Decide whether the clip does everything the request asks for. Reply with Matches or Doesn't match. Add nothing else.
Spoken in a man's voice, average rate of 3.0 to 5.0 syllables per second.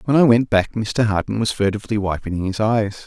Doesn't match